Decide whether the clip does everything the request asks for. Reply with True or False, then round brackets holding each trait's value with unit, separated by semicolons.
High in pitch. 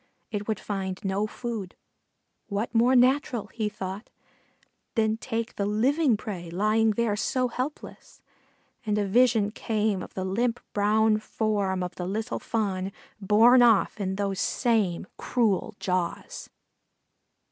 True (215 Hz)